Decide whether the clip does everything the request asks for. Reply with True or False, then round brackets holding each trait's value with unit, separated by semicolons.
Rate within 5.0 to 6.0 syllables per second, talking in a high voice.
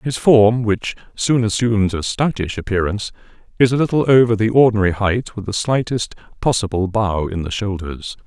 False (5.3 syllables/s; 110 Hz)